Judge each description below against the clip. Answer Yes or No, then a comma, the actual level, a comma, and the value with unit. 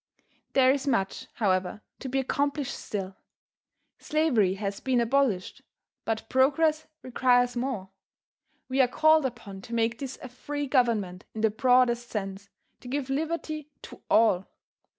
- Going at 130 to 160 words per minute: Yes, average, 140 wpm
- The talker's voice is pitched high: Yes, high, 245 Hz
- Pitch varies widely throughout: No, average, 4.3 semitones